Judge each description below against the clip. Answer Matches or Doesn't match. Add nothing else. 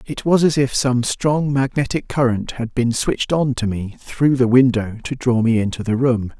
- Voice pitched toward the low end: Matches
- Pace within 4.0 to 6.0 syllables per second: Matches